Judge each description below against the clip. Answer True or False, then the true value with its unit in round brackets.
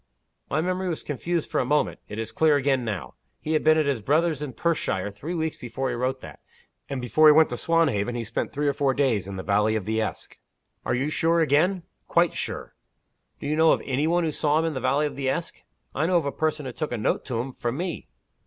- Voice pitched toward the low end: False (145 Hz)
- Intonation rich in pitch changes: False (4.6 semitones)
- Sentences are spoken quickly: True (255 wpm)